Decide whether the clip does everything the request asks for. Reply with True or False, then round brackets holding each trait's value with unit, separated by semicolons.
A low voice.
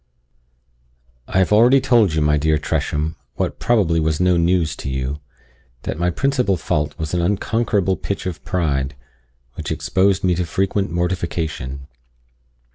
True (85 Hz)